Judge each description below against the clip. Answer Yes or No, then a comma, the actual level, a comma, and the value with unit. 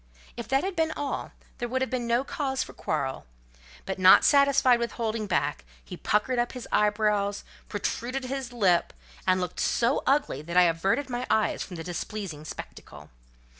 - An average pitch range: No, wide, 5.8 semitones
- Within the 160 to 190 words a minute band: Yes, average, 175 wpm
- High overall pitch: Yes, high, 235 Hz